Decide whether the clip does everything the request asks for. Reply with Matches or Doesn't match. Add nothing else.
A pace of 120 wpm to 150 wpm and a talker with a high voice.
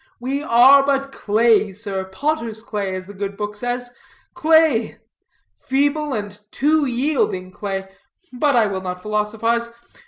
Matches